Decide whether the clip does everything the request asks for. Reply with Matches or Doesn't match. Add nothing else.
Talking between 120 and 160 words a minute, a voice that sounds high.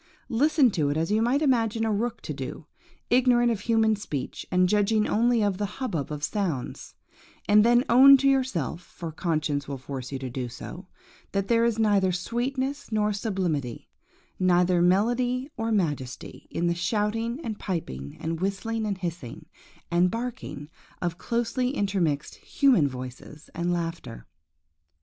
Matches